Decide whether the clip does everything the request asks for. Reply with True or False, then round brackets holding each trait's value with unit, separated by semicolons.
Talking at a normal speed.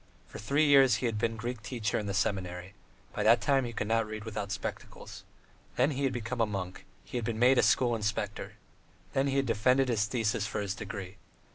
False (220 wpm)